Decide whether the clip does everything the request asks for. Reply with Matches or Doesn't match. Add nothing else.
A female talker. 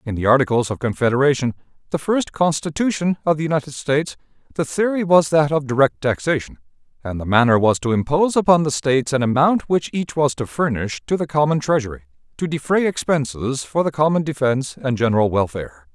Doesn't match